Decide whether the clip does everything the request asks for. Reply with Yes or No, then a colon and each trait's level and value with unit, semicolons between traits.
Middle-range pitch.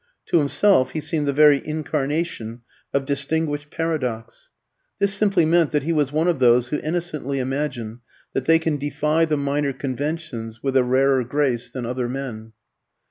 Yes: medium, 145 Hz